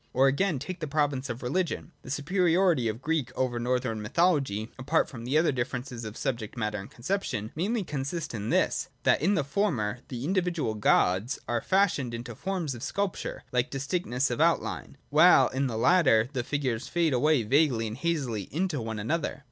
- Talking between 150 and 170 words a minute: No, average, 180 wpm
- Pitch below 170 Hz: Yes, low, 135 Hz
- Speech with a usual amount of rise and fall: No, wide, 5.8 semitones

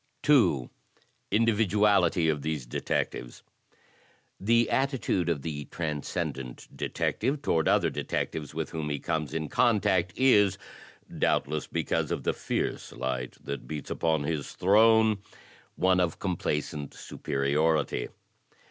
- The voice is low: Yes, very low, 80 Hz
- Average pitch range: No, wide, 6.1 semitones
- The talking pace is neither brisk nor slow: No, slow, 120 wpm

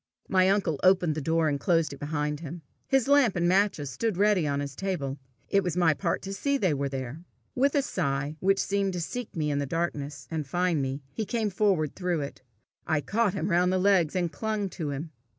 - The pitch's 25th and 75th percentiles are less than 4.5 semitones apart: No, average, 4.9 semitones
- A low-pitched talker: No, medium, 175 Hz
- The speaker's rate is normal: No, fast, 220 wpm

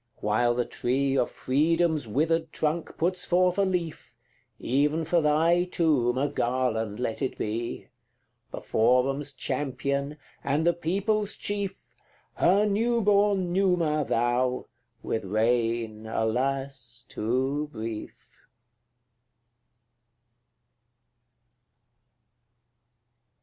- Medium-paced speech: No, slow, 95 wpm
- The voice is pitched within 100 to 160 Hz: Yes, medium, 140 Hz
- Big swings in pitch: Yes, wide, 5.9 semitones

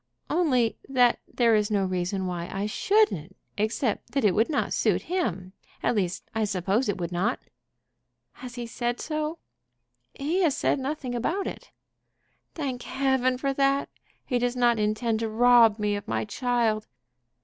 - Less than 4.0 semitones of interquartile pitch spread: No, average, 4.4 semitones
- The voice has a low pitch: No, high, 240 Hz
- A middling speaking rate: Yes, average, 160 wpm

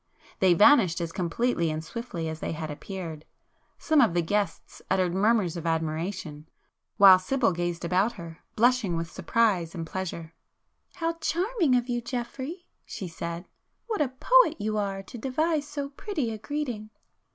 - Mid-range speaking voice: No, high, 195 Hz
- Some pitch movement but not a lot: No, wide, 7.1 semitones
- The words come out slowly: No, average, 165 wpm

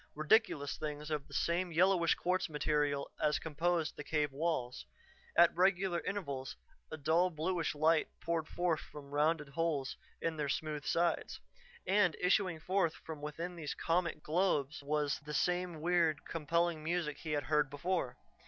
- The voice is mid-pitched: Yes, medium, 160 Hz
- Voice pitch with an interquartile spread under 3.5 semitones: Yes, average, 2.8 semitones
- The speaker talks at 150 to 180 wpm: Yes, average, 155 wpm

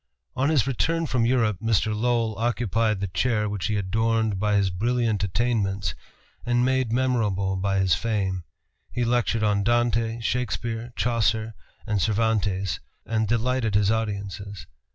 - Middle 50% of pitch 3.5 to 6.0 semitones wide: No, average, 3.0 semitones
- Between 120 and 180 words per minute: Yes, average, 140 wpm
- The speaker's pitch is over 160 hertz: No, low, 110 Hz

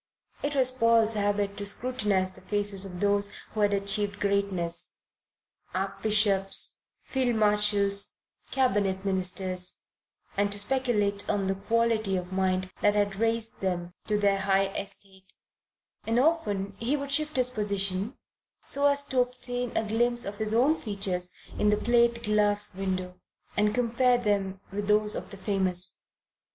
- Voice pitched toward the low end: No, high, 205 Hz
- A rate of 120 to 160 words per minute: Yes, average, 145 wpm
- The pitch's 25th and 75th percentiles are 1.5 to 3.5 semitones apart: Yes, average, 3.0 semitones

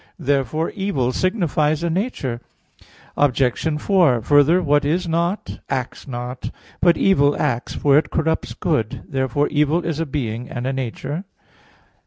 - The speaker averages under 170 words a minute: Yes, average, 140 wpm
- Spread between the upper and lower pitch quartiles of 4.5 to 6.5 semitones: No, average, 4.1 semitones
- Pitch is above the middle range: No, medium, 145 Hz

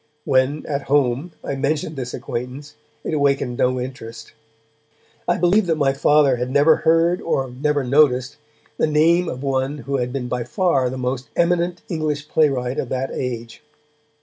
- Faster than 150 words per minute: Yes, average, 165 wpm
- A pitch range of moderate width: Yes, average, 3.3 semitones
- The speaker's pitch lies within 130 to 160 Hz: Yes, medium, 140 Hz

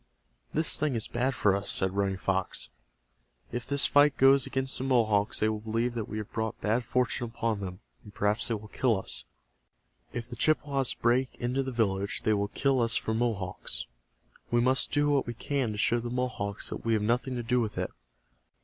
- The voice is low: Yes, low, 115 Hz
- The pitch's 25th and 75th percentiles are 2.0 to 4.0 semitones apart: Yes, average, 3.5 semitones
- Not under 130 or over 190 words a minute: No, fast, 205 wpm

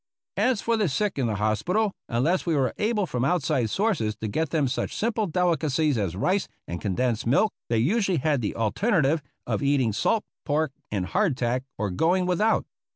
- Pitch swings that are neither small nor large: No, wide, 8.2 semitones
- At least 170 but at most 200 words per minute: Yes, average, 180 wpm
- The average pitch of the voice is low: No, medium, 150 Hz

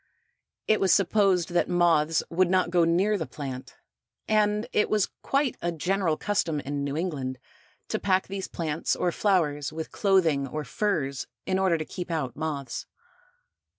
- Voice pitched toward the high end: No, medium, 170 Hz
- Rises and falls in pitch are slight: No, average, 4.3 semitones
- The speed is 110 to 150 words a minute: No, average, 160 wpm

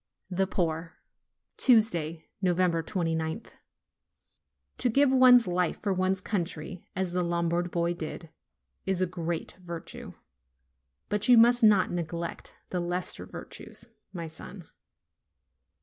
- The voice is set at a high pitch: No, medium, 180 Hz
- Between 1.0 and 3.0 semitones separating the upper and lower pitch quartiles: Yes, narrow, 2.4 semitones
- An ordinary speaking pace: No, slow, 115 wpm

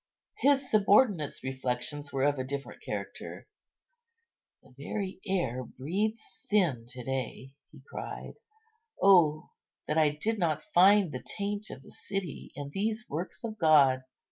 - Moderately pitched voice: Yes, medium, 155 Hz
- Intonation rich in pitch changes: Yes, wide, 6.9 semitones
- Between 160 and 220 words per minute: No, average, 140 wpm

